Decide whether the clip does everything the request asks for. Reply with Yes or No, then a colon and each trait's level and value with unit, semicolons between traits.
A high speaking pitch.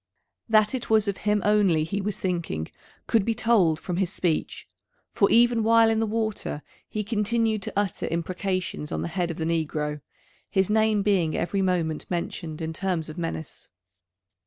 Yes: high, 195 Hz